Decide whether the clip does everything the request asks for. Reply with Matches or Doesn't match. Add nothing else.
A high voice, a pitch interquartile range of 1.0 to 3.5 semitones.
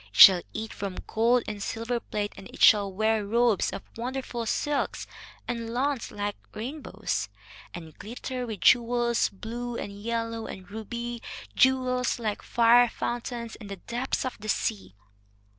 Matches